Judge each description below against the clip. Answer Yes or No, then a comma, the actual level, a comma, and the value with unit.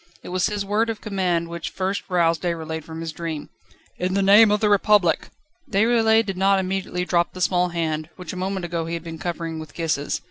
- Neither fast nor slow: No, fast, 215 wpm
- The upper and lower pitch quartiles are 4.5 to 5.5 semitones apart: No, average, 3.0 semitones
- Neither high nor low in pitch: Yes, medium, 180 Hz